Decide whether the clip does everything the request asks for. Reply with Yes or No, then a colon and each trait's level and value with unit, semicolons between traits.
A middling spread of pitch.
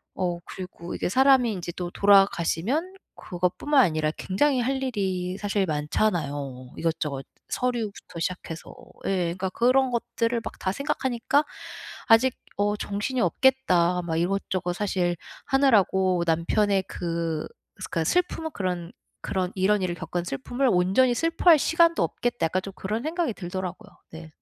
No: wide, 5.8 semitones